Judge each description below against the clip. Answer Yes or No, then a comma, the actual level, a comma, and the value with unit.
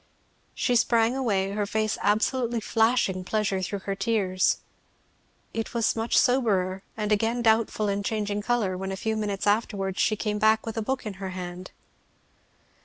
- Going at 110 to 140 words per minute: No, average, 165 wpm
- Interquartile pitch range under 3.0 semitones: Yes, narrow, 2.6 semitones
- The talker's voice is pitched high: Yes, high, 215 Hz